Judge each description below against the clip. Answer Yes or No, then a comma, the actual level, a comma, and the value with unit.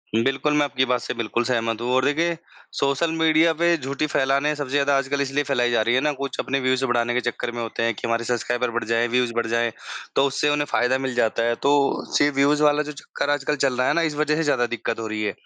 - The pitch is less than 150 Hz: Yes, low, 135 Hz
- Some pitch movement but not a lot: Yes, average, 3.4 semitones